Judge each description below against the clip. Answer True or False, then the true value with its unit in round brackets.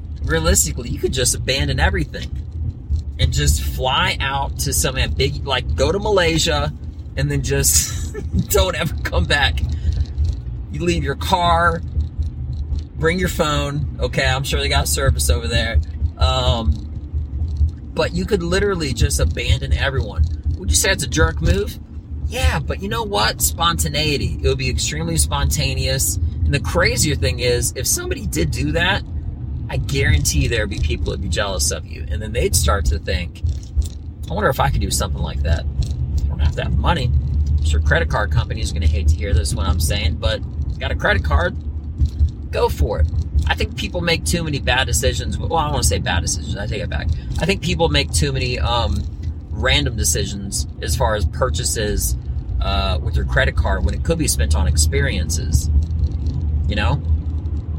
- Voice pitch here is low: True (75 Hz)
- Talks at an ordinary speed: True (185 wpm)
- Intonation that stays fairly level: True (2.1 semitones)